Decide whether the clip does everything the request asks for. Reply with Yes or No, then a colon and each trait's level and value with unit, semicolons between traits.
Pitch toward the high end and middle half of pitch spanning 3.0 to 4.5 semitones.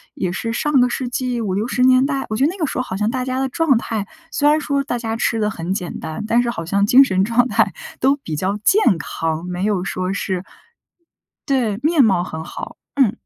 No: high, 230 Hz; wide, 5.6 semitones